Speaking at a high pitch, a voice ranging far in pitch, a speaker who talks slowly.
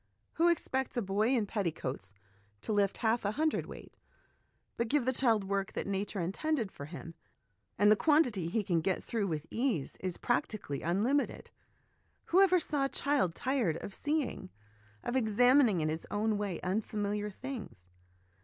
No: high, 210 Hz; wide, 5.7 semitones; average, 160 wpm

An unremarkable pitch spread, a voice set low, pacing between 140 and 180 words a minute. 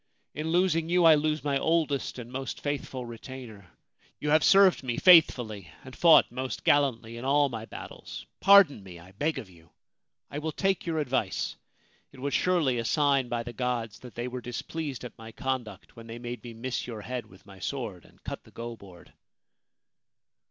No: average, 4.6 semitones; low, 130 Hz; average, 190 wpm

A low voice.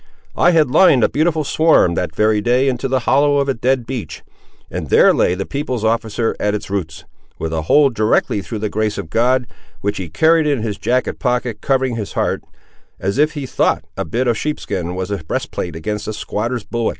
Yes: low, 115 Hz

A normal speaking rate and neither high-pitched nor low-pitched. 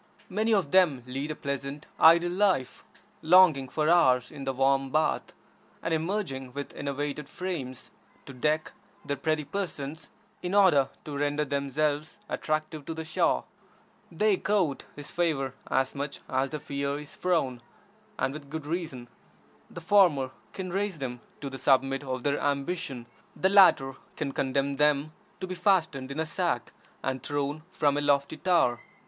Yes: average, 160 wpm; medium, 145 Hz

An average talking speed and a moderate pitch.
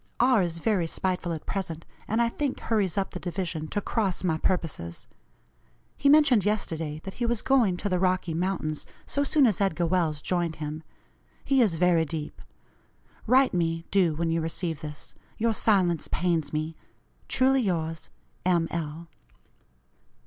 Yes: average, 160 wpm; medium, 175 Hz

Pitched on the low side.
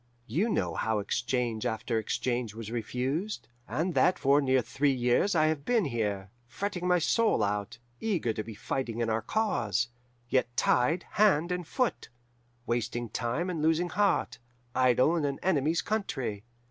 Yes: low, 130 Hz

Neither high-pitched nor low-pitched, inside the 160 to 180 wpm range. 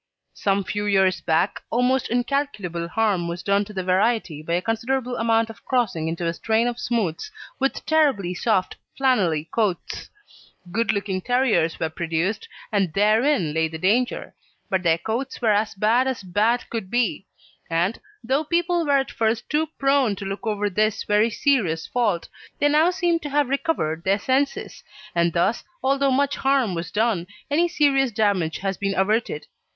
No: high, 215 Hz; average, 170 wpm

